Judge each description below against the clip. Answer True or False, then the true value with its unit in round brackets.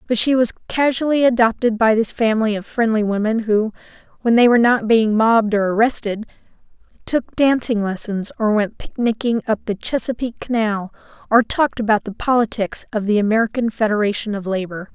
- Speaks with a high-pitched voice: True (225 Hz)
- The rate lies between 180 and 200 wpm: False (165 wpm)